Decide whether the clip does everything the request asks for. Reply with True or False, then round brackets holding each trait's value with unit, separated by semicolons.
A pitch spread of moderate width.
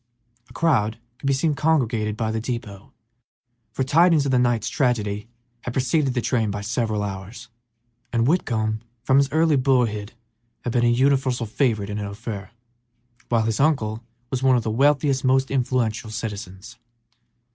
True (3.6 semitones)